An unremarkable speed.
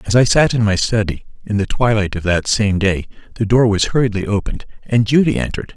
No: fast, 220 wpm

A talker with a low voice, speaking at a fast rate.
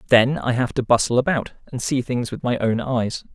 Yes: low, 125 Hz; fast, 235 wpm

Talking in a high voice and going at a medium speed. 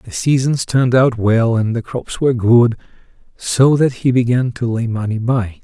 No: low, 120 Hz; average, 190 wpm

